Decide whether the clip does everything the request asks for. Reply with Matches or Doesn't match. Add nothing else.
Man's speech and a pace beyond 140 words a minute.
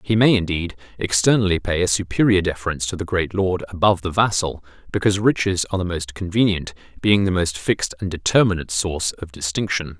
Matches